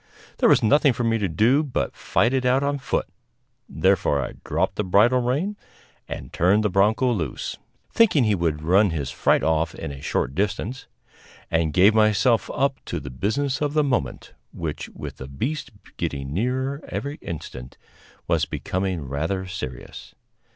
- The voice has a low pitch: Yes, low, 105 Hz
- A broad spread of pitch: Yes, wide, 8.3 semitones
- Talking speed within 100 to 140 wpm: No, average, 165 wpm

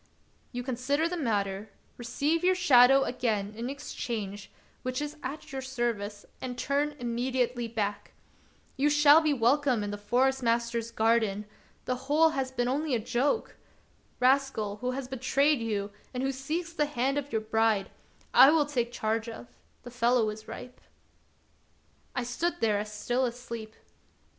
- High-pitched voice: Yes, very high, 250 Hz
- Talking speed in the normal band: Yes, average, 155 wpm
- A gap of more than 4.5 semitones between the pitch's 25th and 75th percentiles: No, average, 3.7 semitones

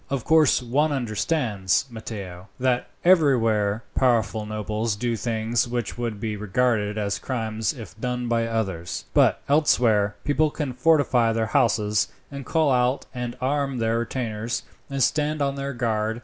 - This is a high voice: No, low, 120 Hz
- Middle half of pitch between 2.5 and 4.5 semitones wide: Yes, average, 3.7 semitones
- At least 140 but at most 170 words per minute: Yes, average, 150 wpm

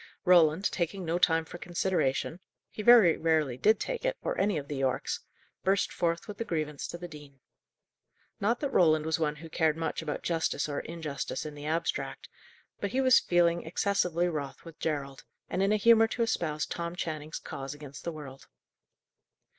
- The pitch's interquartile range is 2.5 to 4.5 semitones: Yes, average, 3.8 semitones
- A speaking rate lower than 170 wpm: No, average, 185 wpm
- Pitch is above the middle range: No, medium, 165 Hz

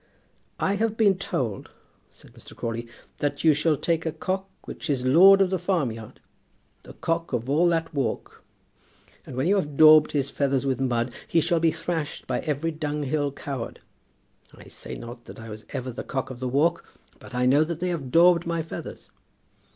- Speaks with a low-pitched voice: No, medium, 150 Hz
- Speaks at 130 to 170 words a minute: No, average, 190 wpm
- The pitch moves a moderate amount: Yes, average, 4.6 semitones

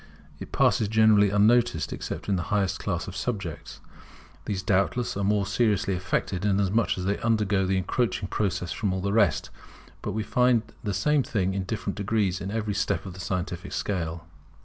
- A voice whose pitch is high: No, low, 100 Hz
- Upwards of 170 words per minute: Yes, average, 180 wpm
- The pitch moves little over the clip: Yes, narrow, 2.3 semitones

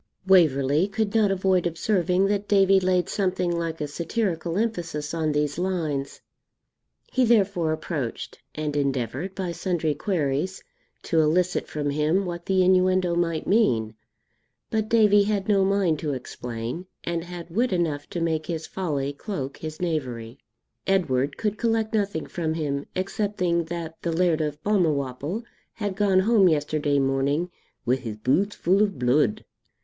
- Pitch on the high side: No, medium, 170 Hz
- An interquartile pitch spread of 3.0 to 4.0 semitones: No, average, 4.6 semitones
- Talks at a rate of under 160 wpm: Yes, average, 150 wpm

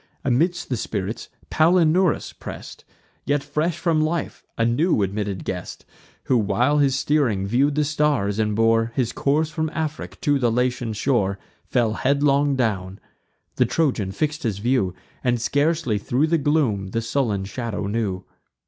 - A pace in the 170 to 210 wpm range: No, average, 150 wpm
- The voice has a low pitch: Yes, low, 125 Hz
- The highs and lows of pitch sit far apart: Yes, wide, 5.9 semitones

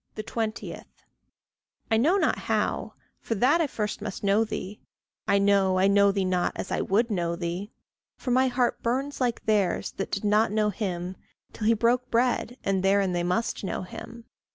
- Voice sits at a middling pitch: No, high, 210 Hz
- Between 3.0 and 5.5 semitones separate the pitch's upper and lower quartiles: Yes, average, 3.4 semitones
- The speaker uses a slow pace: No, average, 180 wpm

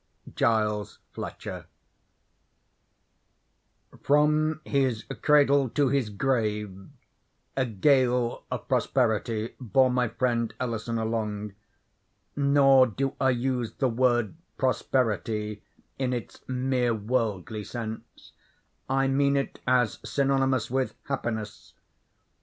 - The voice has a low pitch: Yes, low, 125 Hz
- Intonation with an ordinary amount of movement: Yes, average, 3.3 semitones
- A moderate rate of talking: No, slow, 95 wpm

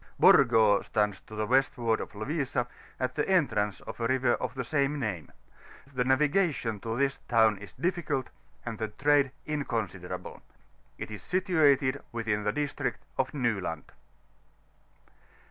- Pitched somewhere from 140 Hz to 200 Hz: No, low, 125 Hz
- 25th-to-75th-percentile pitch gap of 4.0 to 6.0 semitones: Yes, average, 4.8 semitones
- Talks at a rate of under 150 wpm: Yes, average, 140 wpm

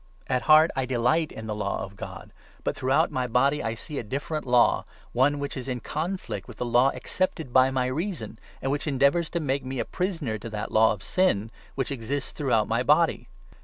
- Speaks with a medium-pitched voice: No, low, 130 Hz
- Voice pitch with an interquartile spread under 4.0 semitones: No, average, 4.3 semitones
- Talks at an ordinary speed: No, fast, 215 wpm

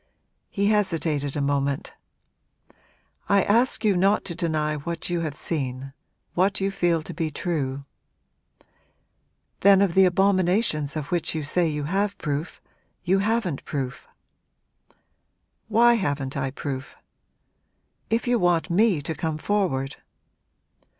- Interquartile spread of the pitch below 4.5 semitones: No, average, 5.3 semitones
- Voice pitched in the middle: Yes, medium, 170 Hz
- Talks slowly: Yes, slow, 130 wpm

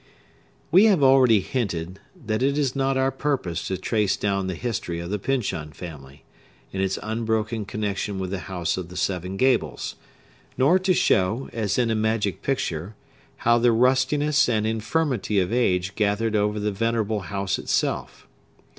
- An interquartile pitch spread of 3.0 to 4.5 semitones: No, average, 5.0 semitones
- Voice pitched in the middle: No, low, 110 Hz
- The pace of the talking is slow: No, average, 165 wpm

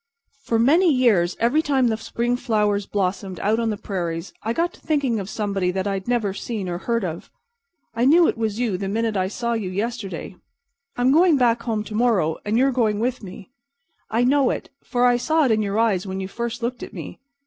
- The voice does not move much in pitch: No, average, 3.8 semitones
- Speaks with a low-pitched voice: No, high, 225 Hz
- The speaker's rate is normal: No, fast, 220 wpm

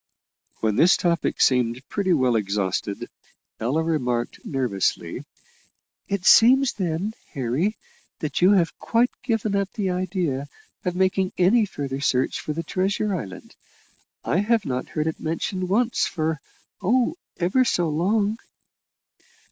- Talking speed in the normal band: No, slow, 130 wpm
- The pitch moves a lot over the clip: Yes, wide, 6.9 semitones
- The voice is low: No, medium, 175 Hz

